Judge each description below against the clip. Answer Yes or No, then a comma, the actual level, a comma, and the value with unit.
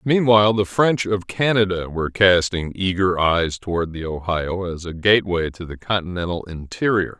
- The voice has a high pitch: No, very low, 95 Hz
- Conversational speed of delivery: Yes, average, 160 wpm